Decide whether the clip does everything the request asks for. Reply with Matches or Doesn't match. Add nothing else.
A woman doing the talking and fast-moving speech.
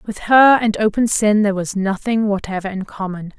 Doesn't match